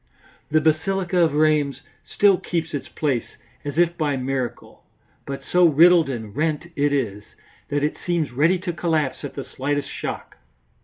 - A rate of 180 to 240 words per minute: No, average, 160 wpm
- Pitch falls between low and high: Yes, medium, 150 Hz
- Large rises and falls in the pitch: No, average, 3.6 semitones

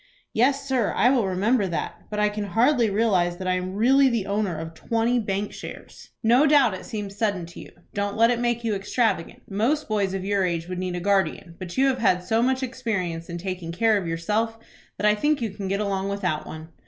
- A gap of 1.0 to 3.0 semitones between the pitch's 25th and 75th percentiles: No, average, 4.0 semitones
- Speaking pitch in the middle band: No, high, 205 Hz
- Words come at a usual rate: No, fast, 230 wpm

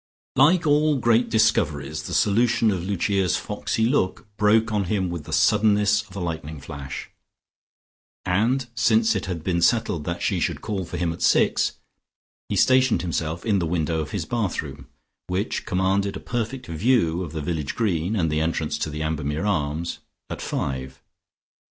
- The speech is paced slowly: No, average, 170 wpm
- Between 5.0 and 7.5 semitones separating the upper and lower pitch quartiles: Yes, wide, 5.5 semitones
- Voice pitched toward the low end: Yes, very low, 95 Hz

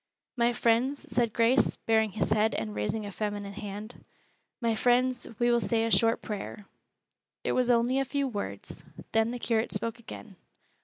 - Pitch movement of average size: No, narrow, 2.2 semitones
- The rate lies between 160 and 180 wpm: Yes, average, 170 wpm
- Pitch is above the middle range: Yes, high, 230 Hz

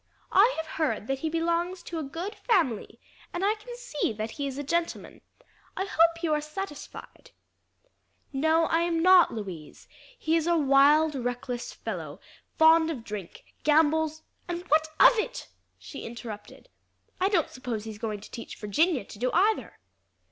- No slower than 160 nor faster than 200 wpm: Yes, average, 170 wpm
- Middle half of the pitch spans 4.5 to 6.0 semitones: Yes, wide, 5.5 semitones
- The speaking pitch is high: Yes, very high, 315 Hz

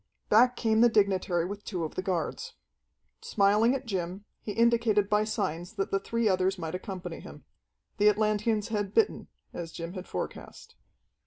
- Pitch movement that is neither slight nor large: Yes, average, 3.1 semitones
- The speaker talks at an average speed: Yes, average, 165 wpm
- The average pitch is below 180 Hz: No, high, 205 Hz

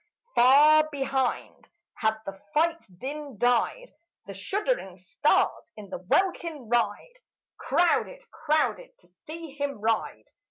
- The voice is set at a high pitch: Yes, very high, 285 Hz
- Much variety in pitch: Yes, wide, 6.8 semitones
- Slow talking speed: Yes, slow, 115 wpm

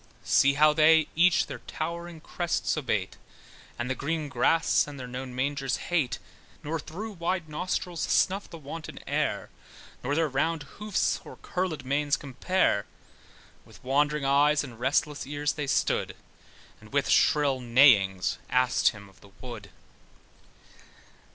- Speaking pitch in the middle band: Yes, medium, 145 Hz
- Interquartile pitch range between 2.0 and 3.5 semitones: No, average, 4.0 semitones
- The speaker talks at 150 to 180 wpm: No, average, 140 wpm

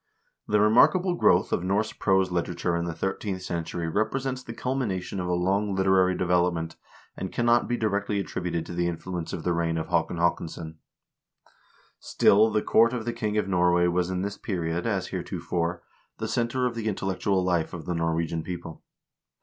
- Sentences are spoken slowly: No, average, 175 wpm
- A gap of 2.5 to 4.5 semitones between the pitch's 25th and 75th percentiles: Yes, average, 3.7 semitones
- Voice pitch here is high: No, very low, 95 Hz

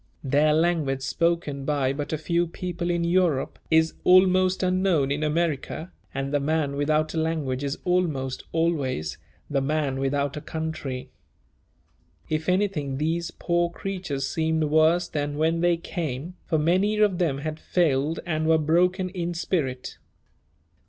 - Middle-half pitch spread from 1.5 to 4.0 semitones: Yes, average, 3.3 semitones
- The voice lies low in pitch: No, medium, 160 Hz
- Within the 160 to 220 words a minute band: No, average, 145 wpm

